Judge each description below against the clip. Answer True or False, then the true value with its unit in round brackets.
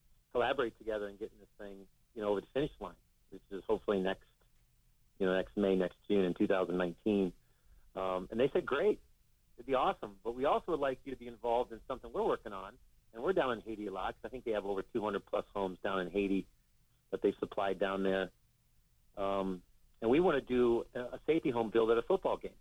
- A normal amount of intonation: True (3.7 semitones)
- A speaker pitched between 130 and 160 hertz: False (100 Hz)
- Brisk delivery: True (225 wpm)